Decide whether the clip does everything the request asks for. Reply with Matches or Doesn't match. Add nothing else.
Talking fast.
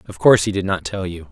Matches